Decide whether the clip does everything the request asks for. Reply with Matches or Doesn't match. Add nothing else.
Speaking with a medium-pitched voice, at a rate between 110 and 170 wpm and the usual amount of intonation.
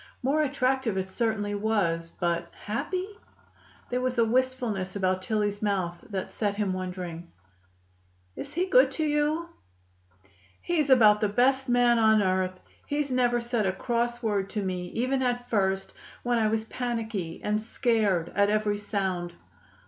Doesn't match